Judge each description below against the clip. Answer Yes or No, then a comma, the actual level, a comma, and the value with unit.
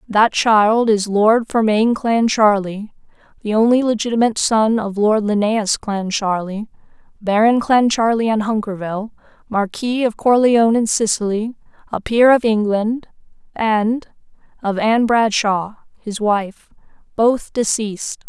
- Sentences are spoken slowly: Yes, slow, 115 wpm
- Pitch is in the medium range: No, high, 220 Hz